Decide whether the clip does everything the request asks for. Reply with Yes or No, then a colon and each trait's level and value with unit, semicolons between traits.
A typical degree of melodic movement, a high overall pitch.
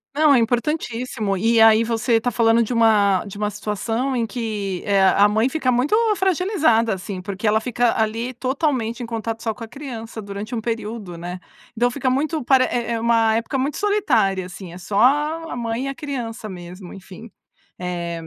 Yes: average, 3.5 semitones; high, 230 Hz